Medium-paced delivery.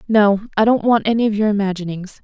No: fast, 215 wpm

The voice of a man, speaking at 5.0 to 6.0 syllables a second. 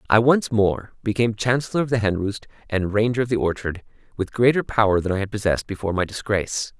No: male; 6.4 syllables/s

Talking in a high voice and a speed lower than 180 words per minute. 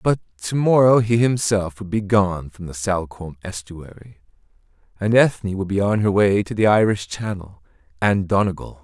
No: low, 100 Hz; average, 170 wpm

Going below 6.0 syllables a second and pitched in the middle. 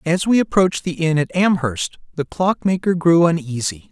Yes: 5.0 syllables/s; medium, 165 Hz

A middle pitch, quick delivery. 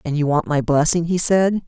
Yes: medium, 160 Hz; fast, 250 wpm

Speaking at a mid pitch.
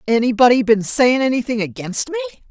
No: very high, 250 Hz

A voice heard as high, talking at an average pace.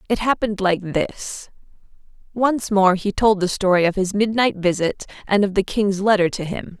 Yes: high, 200 Hz; average, 185 wpm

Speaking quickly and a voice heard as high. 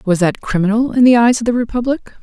Yes: fast, 245 wpm; high, 225 Hz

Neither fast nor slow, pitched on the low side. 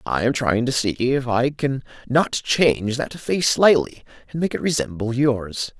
Yes: average, 185 wpm; low, 125 Hz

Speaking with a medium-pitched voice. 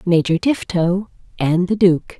Yes: medium, 180 Hz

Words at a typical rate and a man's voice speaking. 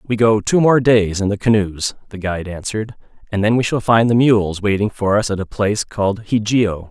No: fast, 225 wpm; male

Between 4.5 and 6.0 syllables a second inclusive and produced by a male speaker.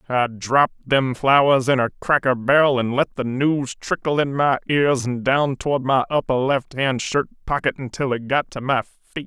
Yes: 4.9 syllables/s; male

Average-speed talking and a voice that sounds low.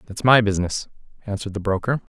Yes: average, 170 wpm; low, 105 Hz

